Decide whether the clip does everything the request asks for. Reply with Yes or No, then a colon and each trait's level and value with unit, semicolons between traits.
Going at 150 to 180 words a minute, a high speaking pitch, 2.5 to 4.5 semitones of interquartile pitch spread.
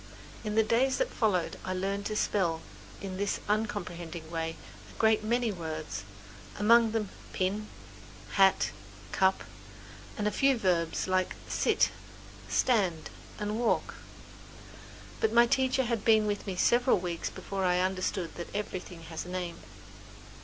No: average, 140 wpm; high, 200 Hz; average, 3.6 semitones